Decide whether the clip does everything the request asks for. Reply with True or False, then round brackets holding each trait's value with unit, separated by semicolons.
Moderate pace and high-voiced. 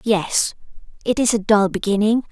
True (155 wpm; 215 Hz)